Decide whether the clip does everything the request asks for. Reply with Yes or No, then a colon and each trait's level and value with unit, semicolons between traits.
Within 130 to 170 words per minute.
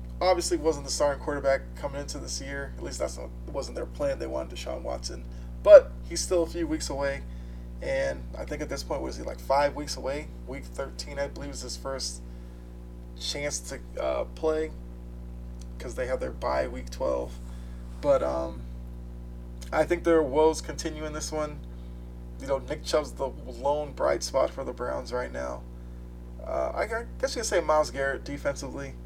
No: average, 180 wpm